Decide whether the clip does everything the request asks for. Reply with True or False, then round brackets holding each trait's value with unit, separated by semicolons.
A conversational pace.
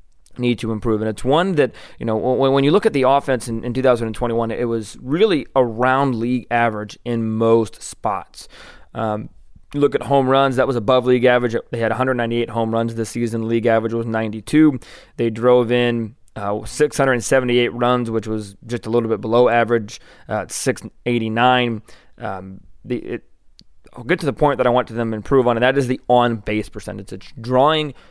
True (190 wpm)